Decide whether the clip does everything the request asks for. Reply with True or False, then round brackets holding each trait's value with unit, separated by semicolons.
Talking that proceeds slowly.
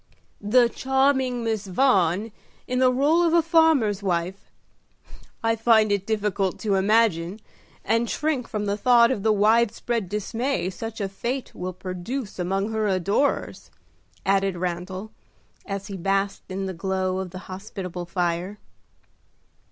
False (145 wpm)